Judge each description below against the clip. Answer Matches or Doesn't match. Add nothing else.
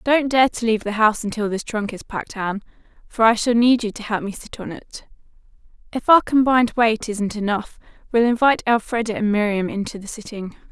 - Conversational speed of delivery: Doesn't match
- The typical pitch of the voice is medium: Doesn't match